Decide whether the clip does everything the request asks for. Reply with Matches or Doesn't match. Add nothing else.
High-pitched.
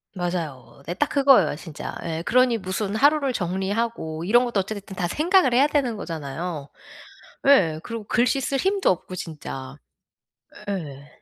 Matches